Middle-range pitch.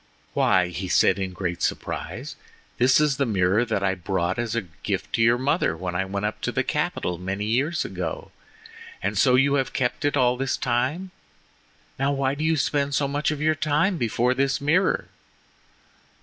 No: low, 125 Hz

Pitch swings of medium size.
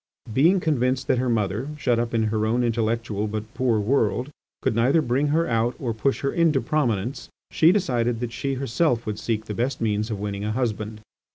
Yes: average, 3.6 semitones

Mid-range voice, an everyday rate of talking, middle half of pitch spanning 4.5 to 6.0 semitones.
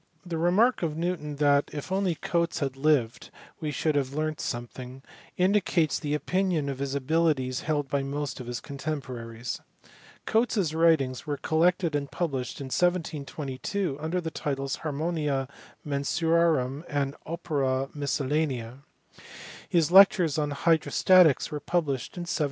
No: medium, 150 Hz; average, 145 wpm; average, 3.5 semitones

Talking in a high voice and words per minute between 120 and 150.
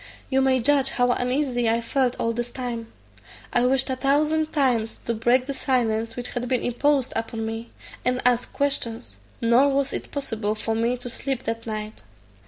No: high, 245 Hz; average, 185 wpm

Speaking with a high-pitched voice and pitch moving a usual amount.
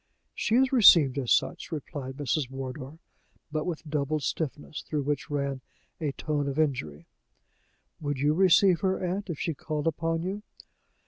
No: medium, 150 Hz; average, 3.1 semitones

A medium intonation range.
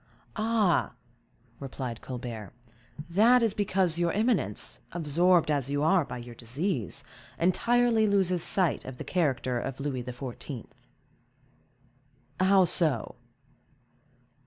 No: wide, 7.0 semitones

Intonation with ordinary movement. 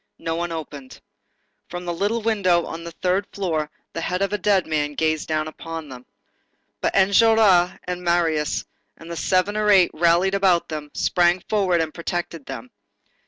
Yes: average, 3.0 semitones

